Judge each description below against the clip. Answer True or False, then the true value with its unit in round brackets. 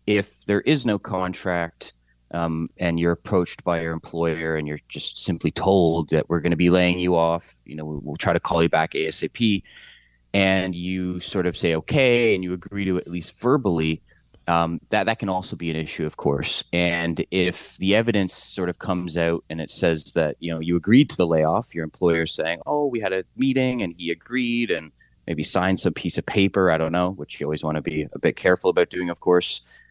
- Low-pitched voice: True (90 Hz)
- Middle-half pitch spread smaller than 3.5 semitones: True (2.5 semitones)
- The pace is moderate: False (225 wpm)